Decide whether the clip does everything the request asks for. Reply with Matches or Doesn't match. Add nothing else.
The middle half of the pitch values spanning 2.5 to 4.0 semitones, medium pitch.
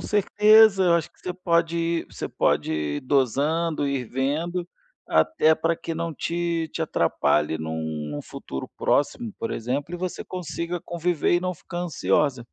Doesn't match